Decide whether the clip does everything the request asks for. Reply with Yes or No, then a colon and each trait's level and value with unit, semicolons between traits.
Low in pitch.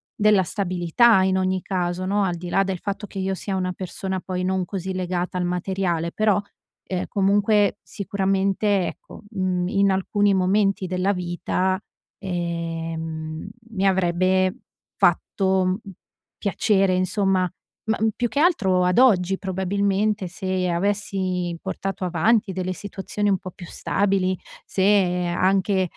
No: high, 190 Hz